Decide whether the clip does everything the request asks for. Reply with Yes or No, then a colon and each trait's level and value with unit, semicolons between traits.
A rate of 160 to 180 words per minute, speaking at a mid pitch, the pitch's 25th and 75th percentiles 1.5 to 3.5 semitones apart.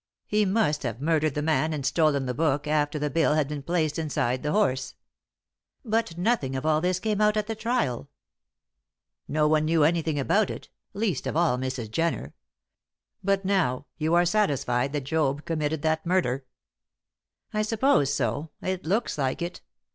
No: average, 170 wpm; medium, 155 Hz; average, 4.6 semitones